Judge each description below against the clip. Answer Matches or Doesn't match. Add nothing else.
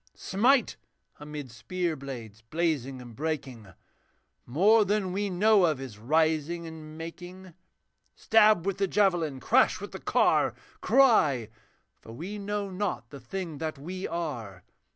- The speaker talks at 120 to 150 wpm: Matches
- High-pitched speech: Doesn't match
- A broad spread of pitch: Matches